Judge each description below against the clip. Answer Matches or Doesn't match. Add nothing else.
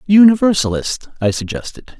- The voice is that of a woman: Doesn't match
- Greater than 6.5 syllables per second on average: Doesn't match